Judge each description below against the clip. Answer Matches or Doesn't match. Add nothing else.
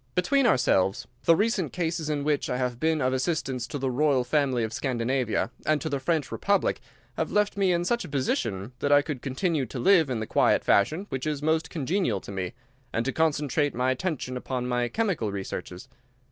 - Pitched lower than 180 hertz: Matches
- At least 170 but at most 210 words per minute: Matches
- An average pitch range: Matches